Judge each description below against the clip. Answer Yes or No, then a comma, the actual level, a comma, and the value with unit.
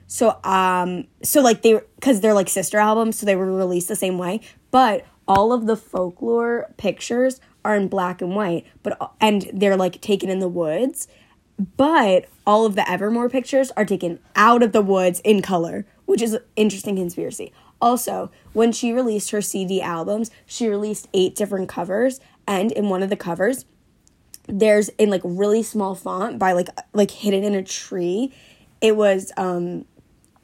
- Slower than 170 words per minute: No, average, 175 wpm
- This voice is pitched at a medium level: No, high, 205 Hz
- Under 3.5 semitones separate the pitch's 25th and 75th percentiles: Yes, average, 2.9 semitones